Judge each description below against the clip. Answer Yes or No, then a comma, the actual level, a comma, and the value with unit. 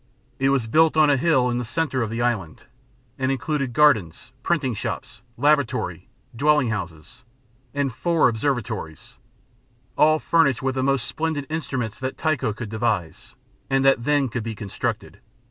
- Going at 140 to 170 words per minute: Yes, average, 155 wpm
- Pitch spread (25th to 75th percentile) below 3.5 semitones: No, average, 4.7 semitones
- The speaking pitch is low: Yes, low, 130 Hz